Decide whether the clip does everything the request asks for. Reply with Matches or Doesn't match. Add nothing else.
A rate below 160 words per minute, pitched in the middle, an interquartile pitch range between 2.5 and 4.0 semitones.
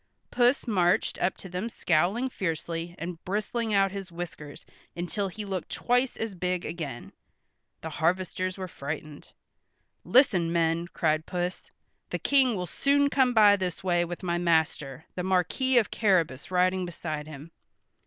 Matches